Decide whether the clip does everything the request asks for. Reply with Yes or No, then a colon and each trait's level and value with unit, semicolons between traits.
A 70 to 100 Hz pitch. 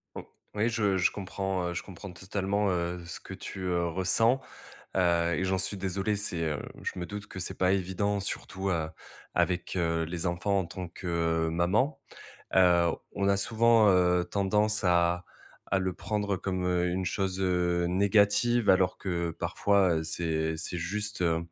Yes: very low, 95 Hz